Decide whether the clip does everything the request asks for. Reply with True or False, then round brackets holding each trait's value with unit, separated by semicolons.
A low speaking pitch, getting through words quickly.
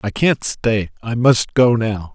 False (115 Hz; 195 wpm)